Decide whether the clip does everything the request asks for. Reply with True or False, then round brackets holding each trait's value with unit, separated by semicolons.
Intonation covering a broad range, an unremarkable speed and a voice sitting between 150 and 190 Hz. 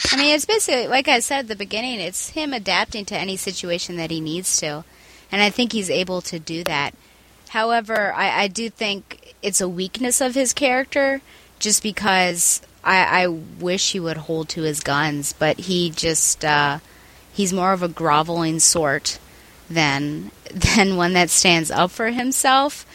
True (5.7 semitones; 180 wpm; 185 Hz)